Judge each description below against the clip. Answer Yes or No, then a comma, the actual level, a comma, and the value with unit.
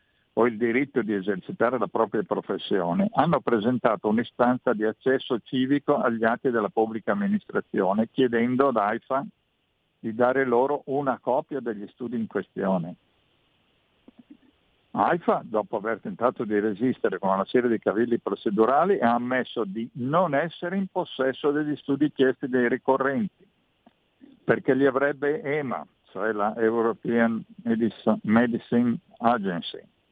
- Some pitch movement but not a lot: Yes, average, 3.4 semitones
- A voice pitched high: No, low, 125 Hz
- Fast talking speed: No, average, 130 wpm